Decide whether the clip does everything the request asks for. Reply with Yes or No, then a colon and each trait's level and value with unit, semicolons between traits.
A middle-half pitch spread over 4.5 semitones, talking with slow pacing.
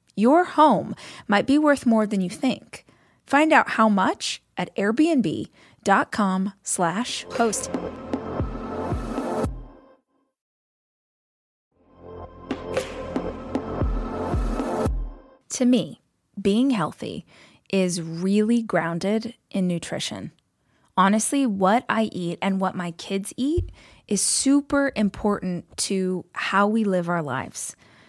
Yes: wide, 5.4 semitones; slow, 95 wpm